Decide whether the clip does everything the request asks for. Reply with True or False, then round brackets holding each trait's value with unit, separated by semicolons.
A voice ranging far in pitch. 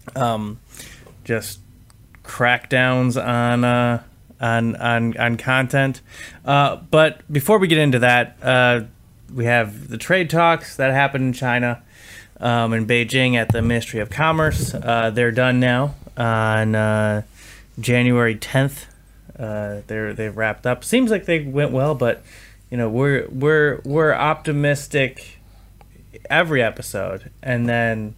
False (3.0 semitones)